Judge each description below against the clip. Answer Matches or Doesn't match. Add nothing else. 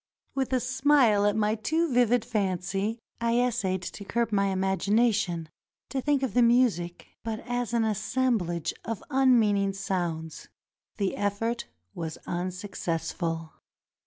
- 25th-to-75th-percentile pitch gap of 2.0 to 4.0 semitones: Doesn't match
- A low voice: Doesn't match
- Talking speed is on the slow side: Matches